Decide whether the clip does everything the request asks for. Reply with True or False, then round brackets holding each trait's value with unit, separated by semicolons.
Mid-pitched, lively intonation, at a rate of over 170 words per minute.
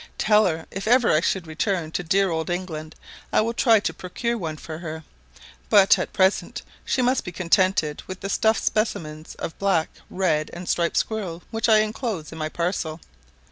False (180 Hz; 4.8 semitones; 190 wpm)